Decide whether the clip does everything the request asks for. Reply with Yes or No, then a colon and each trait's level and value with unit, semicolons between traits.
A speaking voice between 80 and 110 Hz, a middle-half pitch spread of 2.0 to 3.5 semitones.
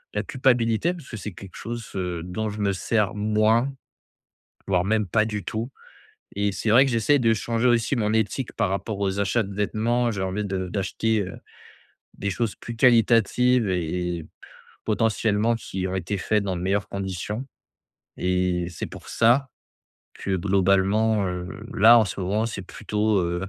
Yes: low, 105 Hz; average, 3.2 semitones